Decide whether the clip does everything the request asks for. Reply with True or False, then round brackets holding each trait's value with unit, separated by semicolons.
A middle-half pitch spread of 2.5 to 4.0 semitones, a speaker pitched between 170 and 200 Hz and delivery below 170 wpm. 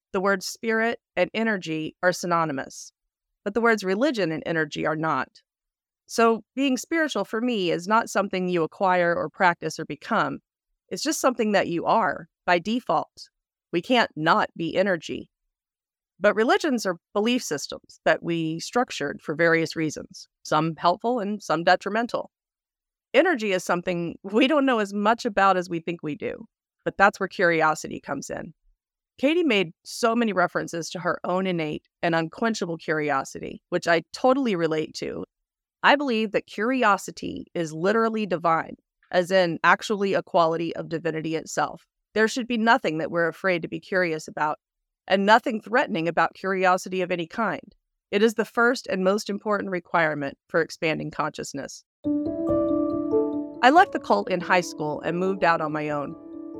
False (5.4 semitones; 190 Hz; 160 wpm)